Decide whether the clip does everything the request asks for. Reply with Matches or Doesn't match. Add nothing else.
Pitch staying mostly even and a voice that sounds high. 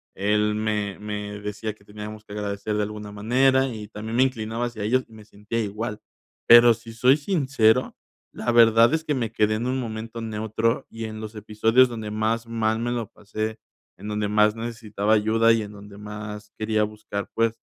Doesn't match